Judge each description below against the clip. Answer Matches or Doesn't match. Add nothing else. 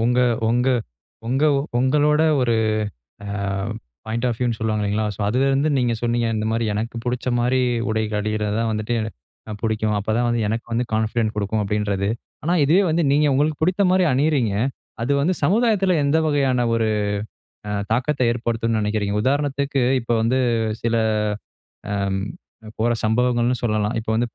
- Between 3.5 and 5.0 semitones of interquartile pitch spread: Matches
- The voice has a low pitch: Matches